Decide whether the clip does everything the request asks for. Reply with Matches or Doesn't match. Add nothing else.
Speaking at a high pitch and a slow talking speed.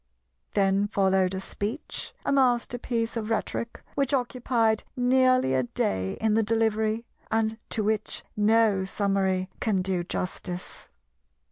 Matches